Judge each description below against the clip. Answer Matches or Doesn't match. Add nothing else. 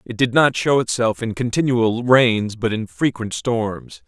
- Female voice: Doesn't match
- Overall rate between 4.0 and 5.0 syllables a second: Matches